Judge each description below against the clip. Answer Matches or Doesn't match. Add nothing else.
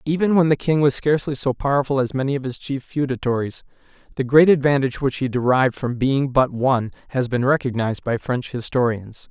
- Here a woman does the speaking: Doesn't match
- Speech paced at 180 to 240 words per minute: Matches